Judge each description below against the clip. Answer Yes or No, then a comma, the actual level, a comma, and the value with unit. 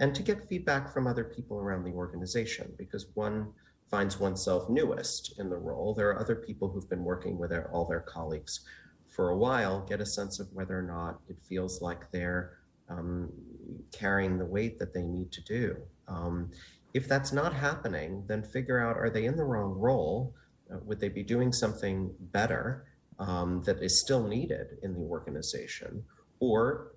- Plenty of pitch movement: No, average, 4.2 semitones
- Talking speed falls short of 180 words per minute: No, average, 185 wpm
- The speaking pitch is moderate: No, low, 100 Hz